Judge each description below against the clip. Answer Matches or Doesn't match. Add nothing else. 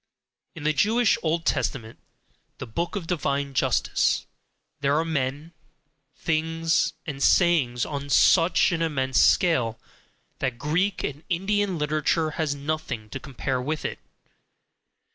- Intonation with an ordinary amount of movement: Matches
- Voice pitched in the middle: Matches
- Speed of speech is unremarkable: Doesn't match